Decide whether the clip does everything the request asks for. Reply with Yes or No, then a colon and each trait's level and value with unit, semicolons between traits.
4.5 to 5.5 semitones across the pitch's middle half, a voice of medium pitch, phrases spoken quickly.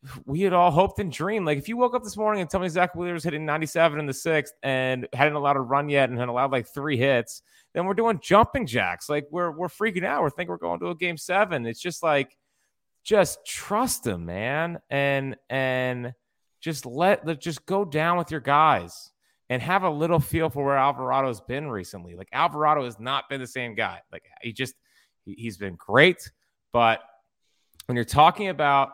Yes: average, 5.2 semitones; medium, 145 Hz; fast, 210 wpm